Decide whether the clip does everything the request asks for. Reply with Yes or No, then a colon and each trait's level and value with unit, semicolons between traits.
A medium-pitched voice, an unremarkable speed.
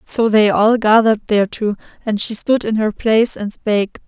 No: high, 215 Hz; average, 190 wpm